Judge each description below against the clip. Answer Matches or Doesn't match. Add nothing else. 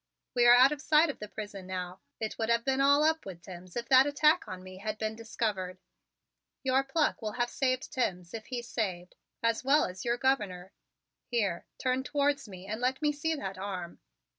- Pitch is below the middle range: Doesn't match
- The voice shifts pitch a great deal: Matches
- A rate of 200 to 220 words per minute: Matches